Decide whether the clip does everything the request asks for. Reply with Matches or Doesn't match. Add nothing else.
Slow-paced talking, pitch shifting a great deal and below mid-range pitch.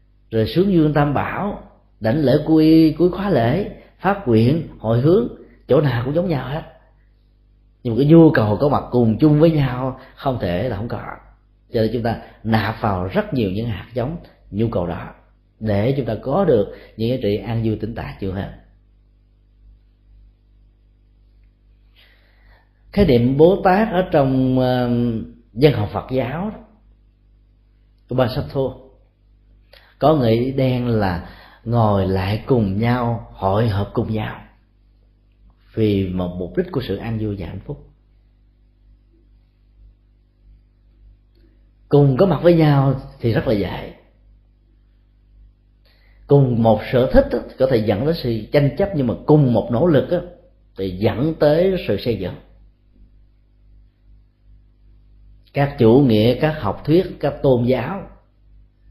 Doesn't match